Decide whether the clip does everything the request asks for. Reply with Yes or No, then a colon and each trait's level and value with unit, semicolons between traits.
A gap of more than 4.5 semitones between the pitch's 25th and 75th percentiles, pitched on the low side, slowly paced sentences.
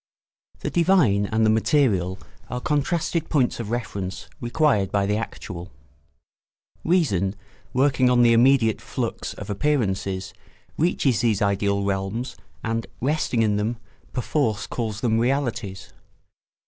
Yes: average, 5.0 semitones; low, 115 Hz; slow, 125 wpm